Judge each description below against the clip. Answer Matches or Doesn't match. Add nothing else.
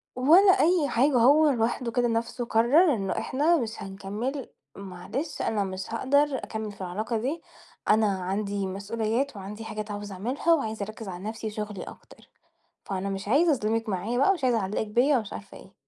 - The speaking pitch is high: Matches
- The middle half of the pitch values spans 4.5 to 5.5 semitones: Matches